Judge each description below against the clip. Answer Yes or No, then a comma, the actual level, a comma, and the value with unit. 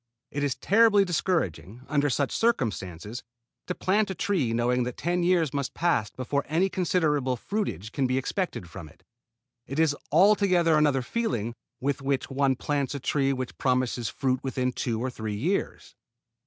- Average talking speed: Yes, average, 165 wpm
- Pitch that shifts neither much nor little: No, wide, 5.7 semitones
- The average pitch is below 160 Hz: Yes, medium, 140 Hz